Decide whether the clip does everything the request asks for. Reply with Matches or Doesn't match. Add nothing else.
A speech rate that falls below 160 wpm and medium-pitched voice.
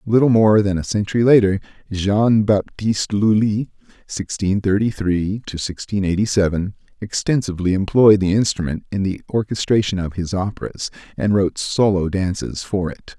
Doesn't match